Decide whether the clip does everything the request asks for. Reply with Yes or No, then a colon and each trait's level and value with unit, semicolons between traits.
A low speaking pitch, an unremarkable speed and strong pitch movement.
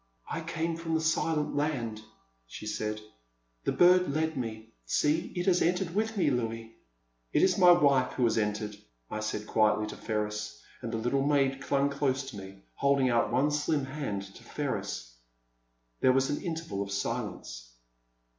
Yes: low, 130 Hz; average, 175 wpm; wide, 6.6 semitones